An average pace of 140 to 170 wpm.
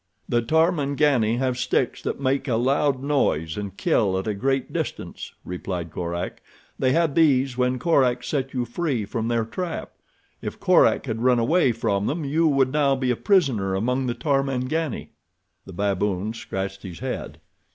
Yes: average, 165 wpm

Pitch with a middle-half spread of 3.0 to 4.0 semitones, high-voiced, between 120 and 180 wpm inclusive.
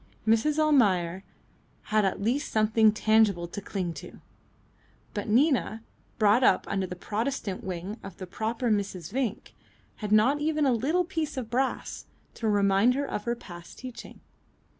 No: average, 4.7 semitones; high, 220 Hz; average, 150 wpm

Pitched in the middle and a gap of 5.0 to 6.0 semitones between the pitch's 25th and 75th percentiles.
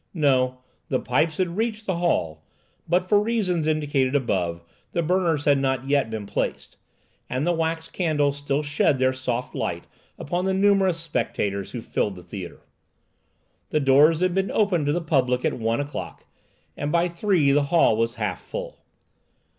Yes: medium, 150 Hz; average, 5.3 semitones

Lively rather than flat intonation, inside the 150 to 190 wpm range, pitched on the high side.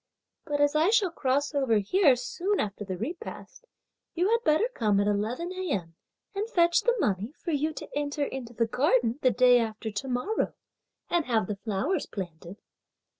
Yes: wide, 7.8 semitones; average, 175 wpm; very high, 265 Hz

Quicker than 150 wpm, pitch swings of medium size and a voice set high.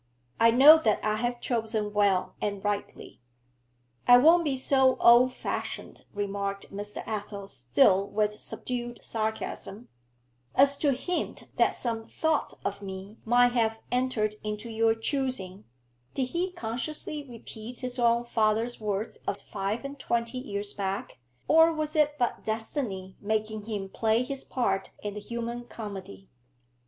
No: average, 145 wpm; average, 3.5 semitones; high, 225 Hz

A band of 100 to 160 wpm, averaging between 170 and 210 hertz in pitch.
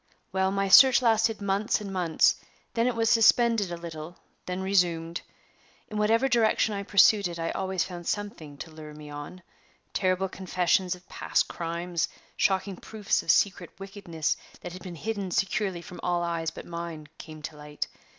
No: average, 170 wpm; medium, 185 Hz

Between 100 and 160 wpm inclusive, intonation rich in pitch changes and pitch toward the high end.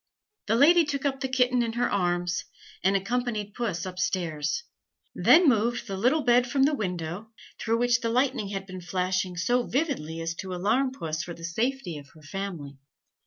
No: average, 185 wpm; wide, 5.8 semitones; high, 210 Hz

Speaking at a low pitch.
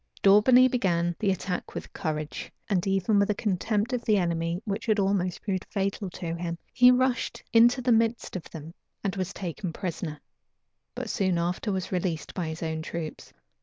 No: high, 190 Hz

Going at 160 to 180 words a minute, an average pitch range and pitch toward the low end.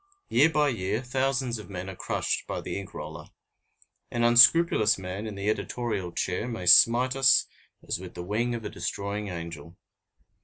Yes: average, 165 wpm; average, 4.4 semitones; low, 110 Hz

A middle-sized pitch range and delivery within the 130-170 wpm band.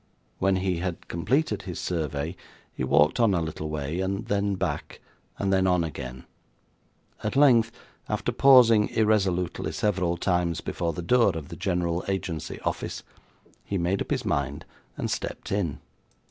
Yes: average, 3.4 semitones; average, 155 wpm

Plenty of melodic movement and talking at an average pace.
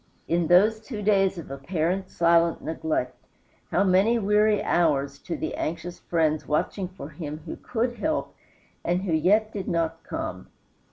No: average, 4.4 semitones; average, 155 wpm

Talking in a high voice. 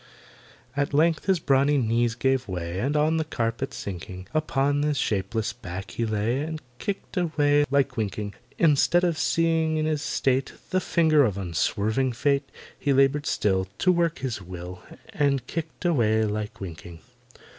No: low, 135 Hz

